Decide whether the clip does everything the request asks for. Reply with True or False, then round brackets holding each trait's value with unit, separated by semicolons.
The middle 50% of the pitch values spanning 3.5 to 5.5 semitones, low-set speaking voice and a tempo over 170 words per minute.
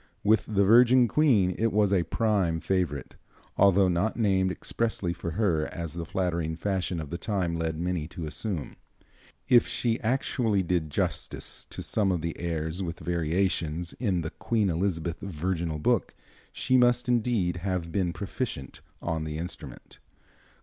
False (4.0 semitones; 90 Hz; 155 wpm)